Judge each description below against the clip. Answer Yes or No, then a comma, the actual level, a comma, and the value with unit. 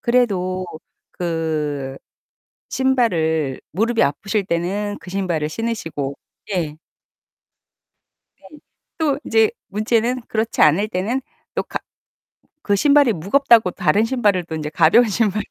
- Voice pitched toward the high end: Yes, high, 200 Hz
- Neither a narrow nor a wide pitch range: No, wide, 6.0 semitones